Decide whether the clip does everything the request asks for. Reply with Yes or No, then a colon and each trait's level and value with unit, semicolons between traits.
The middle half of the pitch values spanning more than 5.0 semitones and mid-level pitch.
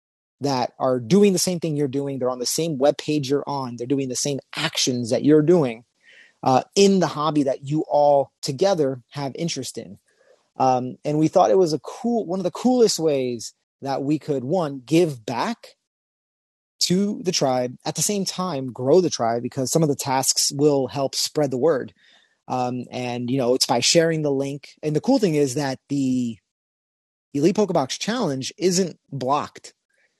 No: average, 4.2 semitones; medium, 145 Hz